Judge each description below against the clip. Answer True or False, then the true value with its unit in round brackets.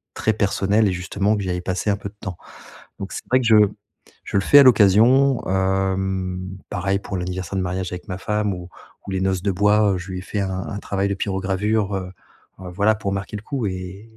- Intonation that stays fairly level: True (1.8 semitones)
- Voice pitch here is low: True (95 Hz)